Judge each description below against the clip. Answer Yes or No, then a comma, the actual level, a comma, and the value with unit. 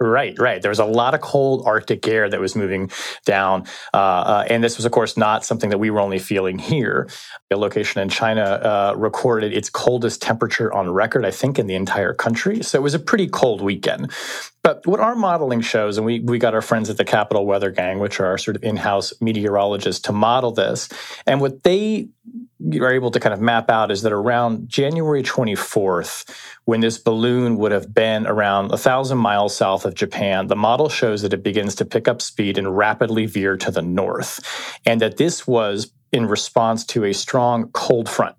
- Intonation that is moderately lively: Yes, average, 3.2 semitones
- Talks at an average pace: No, fast, 210 wpm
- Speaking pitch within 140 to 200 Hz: No, low, 110 Hz